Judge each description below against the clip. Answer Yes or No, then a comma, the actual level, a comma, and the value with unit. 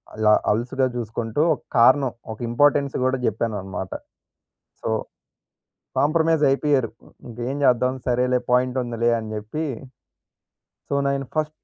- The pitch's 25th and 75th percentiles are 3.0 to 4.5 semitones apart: Yes, average, 3.3 semitones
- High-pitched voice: No, low, 125 Hz